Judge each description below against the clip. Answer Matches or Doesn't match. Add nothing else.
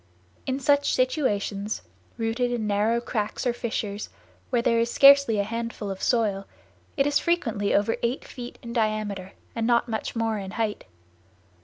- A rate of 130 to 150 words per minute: Doesn't match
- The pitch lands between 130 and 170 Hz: Doesn't match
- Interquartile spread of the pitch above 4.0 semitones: Doesn't match